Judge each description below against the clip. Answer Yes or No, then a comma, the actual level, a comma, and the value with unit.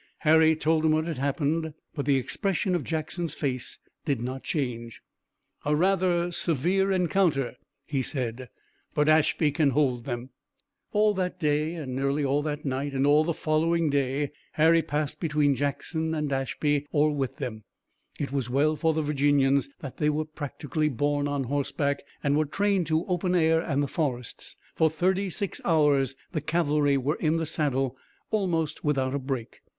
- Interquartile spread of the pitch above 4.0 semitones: No, average, 2.7 semitones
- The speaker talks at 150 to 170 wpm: Yes, average, 165 wpm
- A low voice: No, medium, 150 Hz